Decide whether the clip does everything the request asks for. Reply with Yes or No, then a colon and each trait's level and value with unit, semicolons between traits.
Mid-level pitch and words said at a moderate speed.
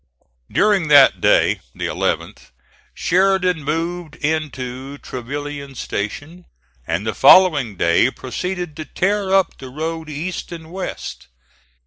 No: medium, 155 Hz; slow, 115 wpm